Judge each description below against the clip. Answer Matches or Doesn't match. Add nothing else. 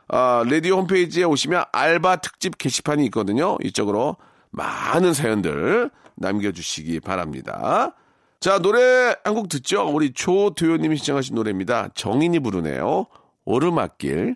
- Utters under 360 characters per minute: Matches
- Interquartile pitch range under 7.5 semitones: Doesn't match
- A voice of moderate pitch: Matches